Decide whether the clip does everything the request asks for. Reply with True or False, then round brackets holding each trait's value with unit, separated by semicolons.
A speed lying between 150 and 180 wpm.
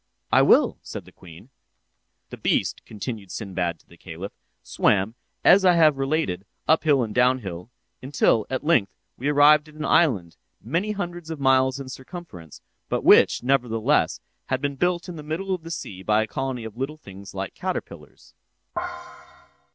True (170 wpm)